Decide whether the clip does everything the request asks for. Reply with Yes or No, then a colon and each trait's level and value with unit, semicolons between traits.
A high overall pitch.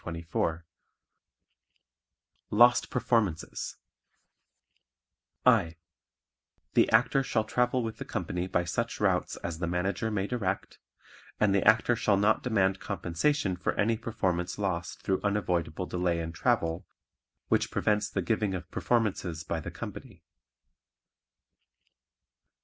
No: low, 100 Hz